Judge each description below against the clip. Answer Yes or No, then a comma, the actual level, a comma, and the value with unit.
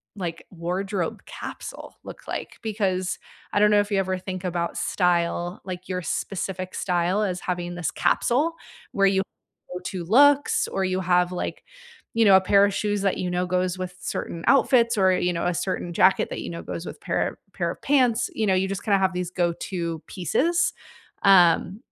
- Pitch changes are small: Yes, narrow, 2.2 semitones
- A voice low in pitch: No, medium, 185 Hz